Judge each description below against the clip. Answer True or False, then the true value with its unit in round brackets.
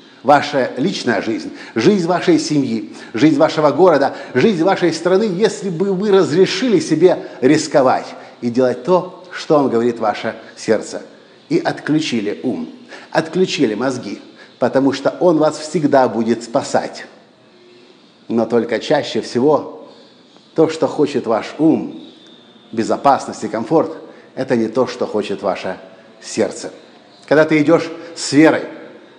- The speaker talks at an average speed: True (125 wpm)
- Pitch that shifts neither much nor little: False (7.0 semitones)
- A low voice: False (155 Hz)